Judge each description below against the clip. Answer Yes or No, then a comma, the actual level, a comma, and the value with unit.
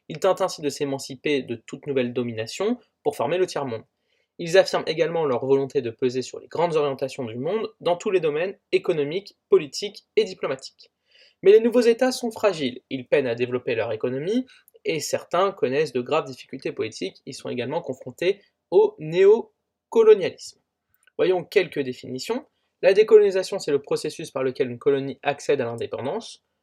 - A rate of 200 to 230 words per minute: No, average, 165 wpm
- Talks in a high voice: Yes, high, 205 Hz